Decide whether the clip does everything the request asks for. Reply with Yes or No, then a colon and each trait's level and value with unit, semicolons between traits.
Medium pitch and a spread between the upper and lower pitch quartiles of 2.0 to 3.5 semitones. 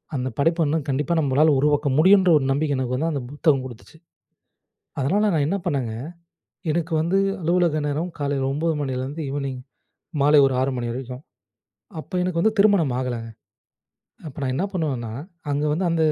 No: medium, 145 Hz; average, 3.9 semitones